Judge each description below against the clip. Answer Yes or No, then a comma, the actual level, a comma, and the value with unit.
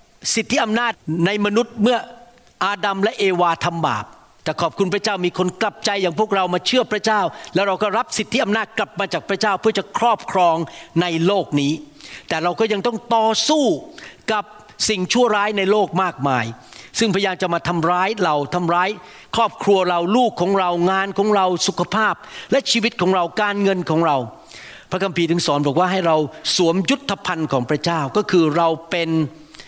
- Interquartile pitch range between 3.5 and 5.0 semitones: Yes, average, 3.9 semitones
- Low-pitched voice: No, high, 195 Hz